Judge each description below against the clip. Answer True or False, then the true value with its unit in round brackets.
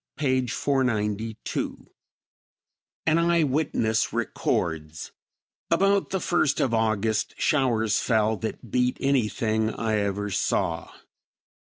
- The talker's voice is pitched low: True (115 Hz)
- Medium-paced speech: False (100 wpm)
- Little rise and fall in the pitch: False (4.4 semitones)